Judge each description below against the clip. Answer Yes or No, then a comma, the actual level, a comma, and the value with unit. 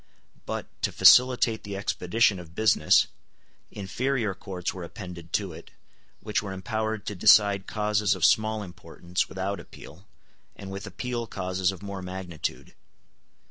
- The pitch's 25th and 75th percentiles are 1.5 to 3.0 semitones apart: Yes, average, 2.7 semitones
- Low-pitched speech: Yes, low, 100 Hz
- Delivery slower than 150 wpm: Yes, average, 140 wpm